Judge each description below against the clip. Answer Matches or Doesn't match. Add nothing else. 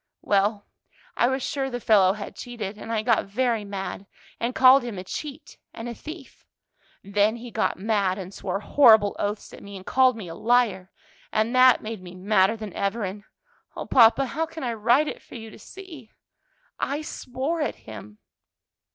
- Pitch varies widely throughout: Doesn't match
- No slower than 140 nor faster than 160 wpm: Doesn't match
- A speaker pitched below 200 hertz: Doesn't match